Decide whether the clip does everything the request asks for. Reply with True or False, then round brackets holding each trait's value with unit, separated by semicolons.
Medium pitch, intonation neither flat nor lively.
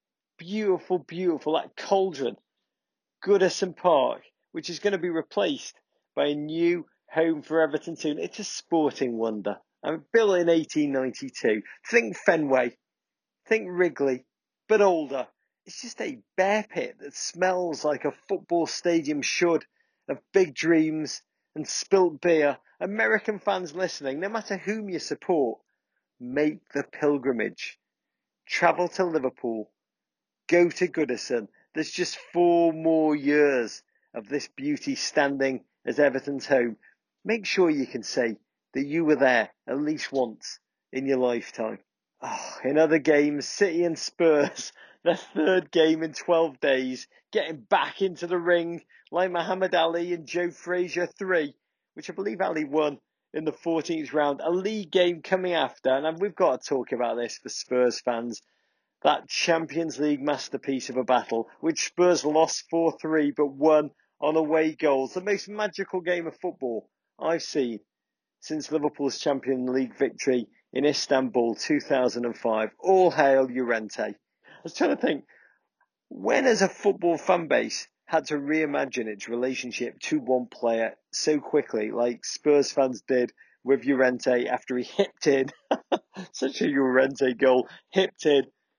True (155 Hz; 4.8 semitones)